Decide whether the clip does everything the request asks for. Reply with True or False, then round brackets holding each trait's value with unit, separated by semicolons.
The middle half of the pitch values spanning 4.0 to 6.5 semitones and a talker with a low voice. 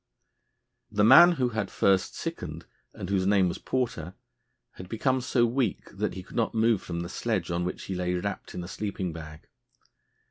True (4.6 semitones; 100 Hz)